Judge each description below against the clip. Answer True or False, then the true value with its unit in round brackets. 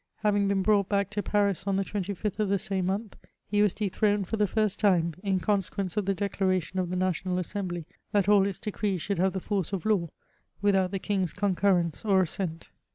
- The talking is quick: True (210 wpm)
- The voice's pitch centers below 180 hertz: False (195 Hz)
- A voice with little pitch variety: True (1.9 semitones)